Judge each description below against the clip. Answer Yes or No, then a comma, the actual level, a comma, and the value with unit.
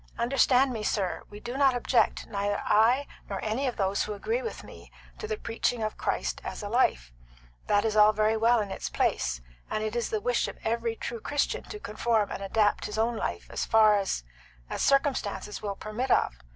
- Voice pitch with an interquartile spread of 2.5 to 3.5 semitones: Yes, average, 2.8 semitones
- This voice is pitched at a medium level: No, high, 220 Hz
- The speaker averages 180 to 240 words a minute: Yes, fast, 205 wpm